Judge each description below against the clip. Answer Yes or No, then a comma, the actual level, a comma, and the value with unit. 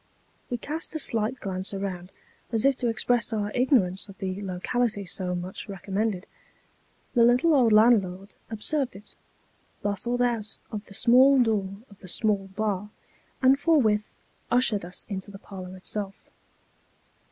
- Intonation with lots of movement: No, average, 4.0 semitones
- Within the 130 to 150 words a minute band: Yes, average, 145 wpm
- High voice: Yes, high, 210 Hz